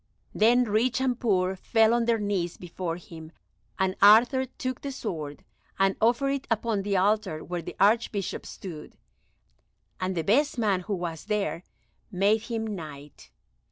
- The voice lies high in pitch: Yes, high, 205 Hz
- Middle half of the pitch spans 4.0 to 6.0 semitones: Yes, average, 4.3 semitones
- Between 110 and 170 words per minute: Yes, average, 155 wpm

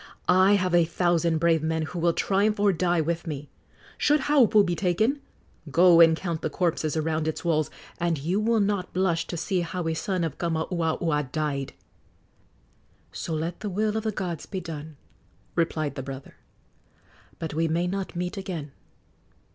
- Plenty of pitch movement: No, average, 2.8 semitones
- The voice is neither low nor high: Yes, medium, 170 Hz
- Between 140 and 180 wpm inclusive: Yes, average, 170 wpm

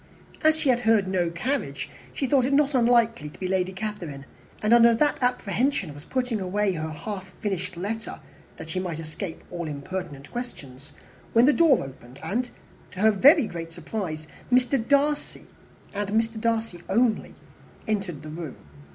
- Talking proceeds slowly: No, average, 165 wpm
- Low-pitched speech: No, high, 205 Hz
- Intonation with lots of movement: Yes, wide, 6.3 semitones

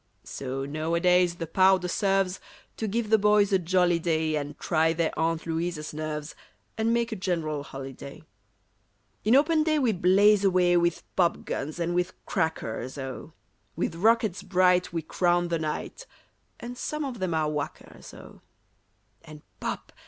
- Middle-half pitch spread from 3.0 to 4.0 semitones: Yes, average, 3.7 semitones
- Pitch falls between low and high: Yes, medium, 175 Hz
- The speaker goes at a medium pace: Yes, average, 150 wpm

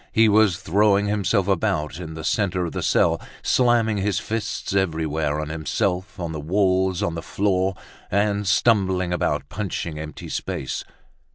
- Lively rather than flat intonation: No, average, 4.0 semitones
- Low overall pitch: Yes, very low, 95 Hz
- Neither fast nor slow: Yes, average, 155 wpm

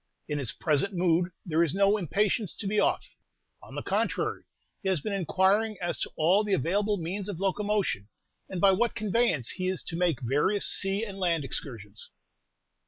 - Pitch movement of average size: Yes, average, 3.9 semitones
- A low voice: No, high, 190 Hz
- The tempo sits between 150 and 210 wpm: Yes, average, 180 wpm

